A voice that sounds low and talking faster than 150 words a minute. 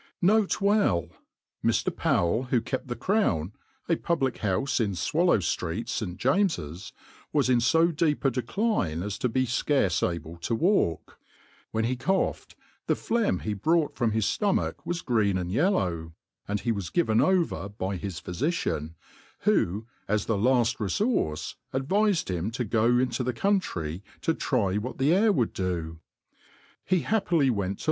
Yes: low, 120 Hz; average, 160 wpm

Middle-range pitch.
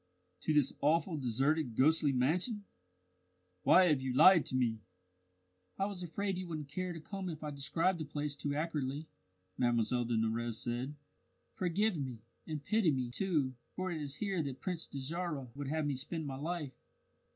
Yes: medium, 150 Hz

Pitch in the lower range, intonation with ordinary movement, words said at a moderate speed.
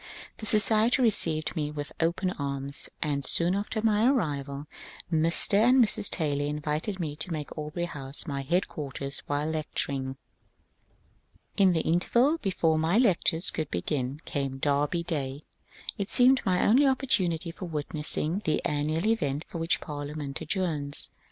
No: medium, 160 Hz; average, 4.7 semitones; average, 145 wpm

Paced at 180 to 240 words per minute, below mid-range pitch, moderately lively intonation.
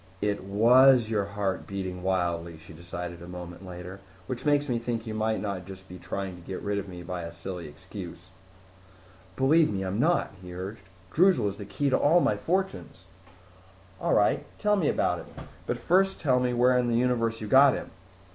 No: average, 200 wpm; low, 100 Hz; wide, 5.7 semitones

